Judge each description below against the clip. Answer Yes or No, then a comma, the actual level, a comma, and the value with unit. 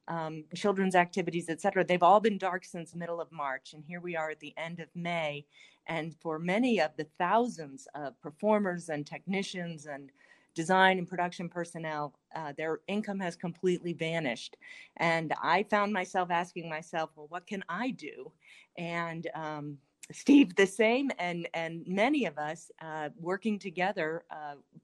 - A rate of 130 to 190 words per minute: Yes, average, 165 wpm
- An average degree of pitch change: Yes, average, 3.2 semitones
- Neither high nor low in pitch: Yes, medium, 170 Hz